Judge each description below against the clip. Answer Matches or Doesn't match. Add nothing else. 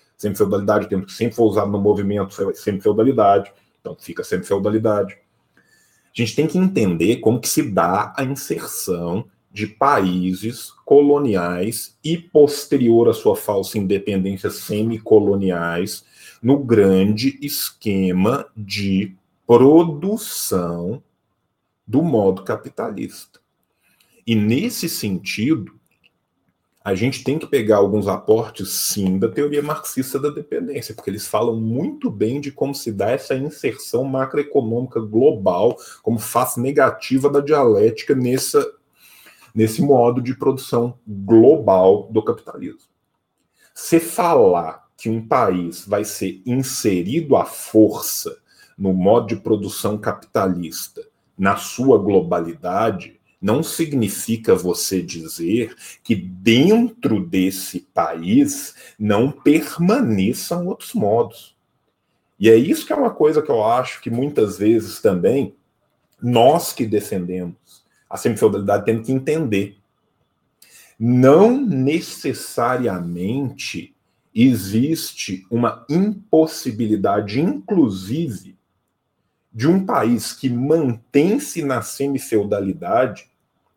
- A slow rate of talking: Matches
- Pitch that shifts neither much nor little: Doesn't match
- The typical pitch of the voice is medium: Doesn't match